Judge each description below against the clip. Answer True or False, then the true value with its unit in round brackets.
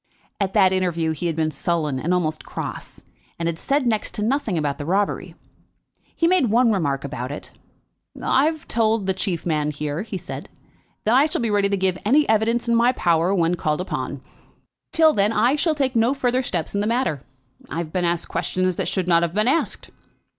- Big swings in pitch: True (6.0 semitones)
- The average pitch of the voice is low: False (190 Hz)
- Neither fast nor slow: False (210 wpm)